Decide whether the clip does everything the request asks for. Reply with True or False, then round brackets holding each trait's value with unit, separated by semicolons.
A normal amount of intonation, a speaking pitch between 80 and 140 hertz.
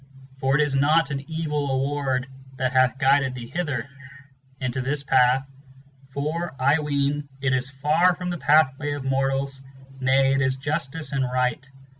False (2.0 semitones; 135 Hz)